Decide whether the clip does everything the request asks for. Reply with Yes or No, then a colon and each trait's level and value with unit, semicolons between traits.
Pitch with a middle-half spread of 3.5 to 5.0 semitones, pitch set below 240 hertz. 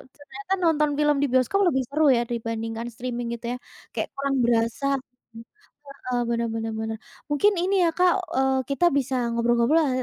No: average, 4.0 semitones; very high, 260 Hz